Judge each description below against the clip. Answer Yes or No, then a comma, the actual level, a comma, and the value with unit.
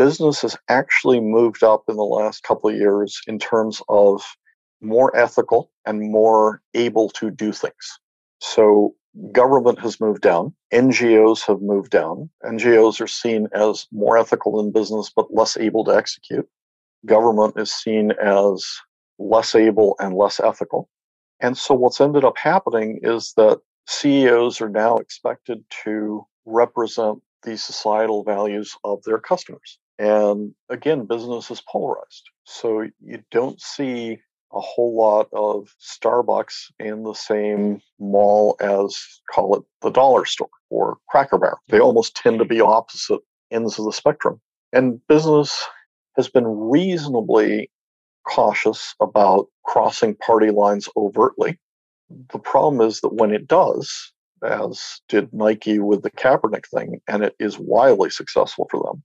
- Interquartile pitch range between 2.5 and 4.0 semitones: Yes, average, 2.8 semitones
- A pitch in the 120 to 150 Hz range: No, low, 110 Hz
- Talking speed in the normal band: Yes, average, 145 wpm